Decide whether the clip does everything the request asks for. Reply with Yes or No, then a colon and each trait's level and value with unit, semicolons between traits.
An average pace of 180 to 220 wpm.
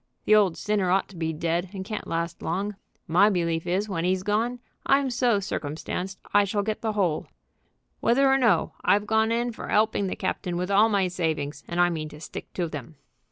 Yes: fast, 205 wpm